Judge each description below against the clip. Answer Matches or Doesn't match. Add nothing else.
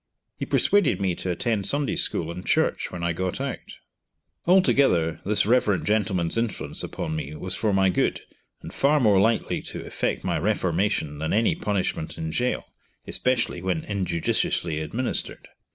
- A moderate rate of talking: Matches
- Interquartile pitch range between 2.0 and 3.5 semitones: Doesn't match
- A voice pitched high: Doesn't match